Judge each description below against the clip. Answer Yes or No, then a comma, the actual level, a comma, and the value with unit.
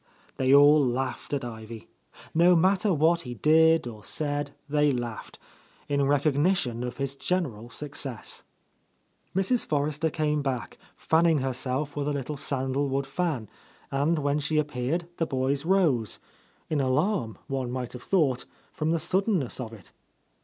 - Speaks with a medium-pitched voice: Yes, medium, 145 Hz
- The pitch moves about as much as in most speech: Yes, average, 3.6 semitones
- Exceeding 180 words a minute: No, average, 150 wpm